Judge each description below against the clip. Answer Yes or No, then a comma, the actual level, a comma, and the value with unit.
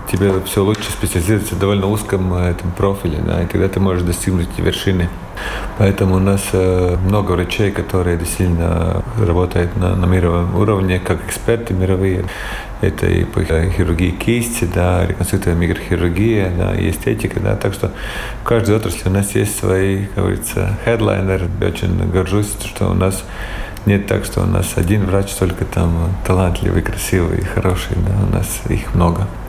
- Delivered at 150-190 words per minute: Yes, fast, 160 wpm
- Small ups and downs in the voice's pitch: Yes, narrow, 2.3 semitones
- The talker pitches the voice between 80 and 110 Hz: Yes, very low, 95 Hz